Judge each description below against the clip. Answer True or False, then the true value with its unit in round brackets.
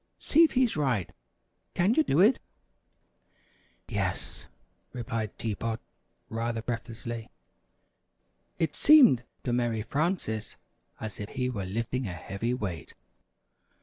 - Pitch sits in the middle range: False (120 Hz)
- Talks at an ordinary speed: False (115 wpm)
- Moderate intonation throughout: True (4.9 semitones)